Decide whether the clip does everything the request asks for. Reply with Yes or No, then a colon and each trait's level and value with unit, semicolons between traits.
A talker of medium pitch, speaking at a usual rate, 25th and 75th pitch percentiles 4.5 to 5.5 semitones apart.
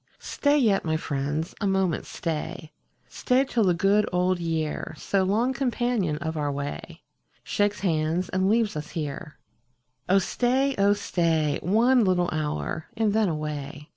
Yes: medium, 180 Hz; average, 155 wpm; average, 5.1 semitones